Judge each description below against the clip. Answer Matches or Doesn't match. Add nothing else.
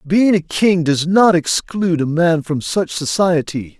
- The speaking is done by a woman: Doesn't match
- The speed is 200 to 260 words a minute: Doesn't match